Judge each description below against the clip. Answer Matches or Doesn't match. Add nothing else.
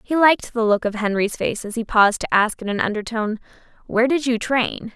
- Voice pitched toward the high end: Matches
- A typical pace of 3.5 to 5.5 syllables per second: Doesn't match